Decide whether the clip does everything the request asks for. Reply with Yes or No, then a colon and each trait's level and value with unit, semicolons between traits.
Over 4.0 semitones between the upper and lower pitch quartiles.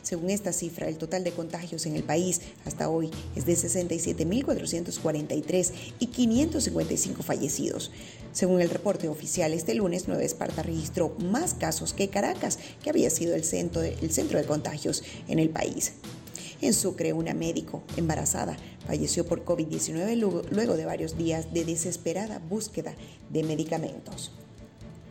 No: narrow, 2.4 semitones